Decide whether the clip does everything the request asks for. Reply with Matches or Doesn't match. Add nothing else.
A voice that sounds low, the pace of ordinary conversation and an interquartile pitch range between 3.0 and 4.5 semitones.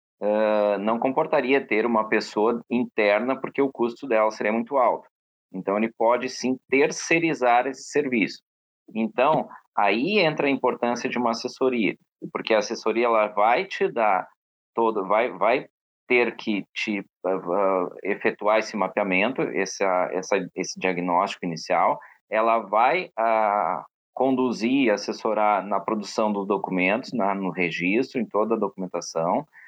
Matches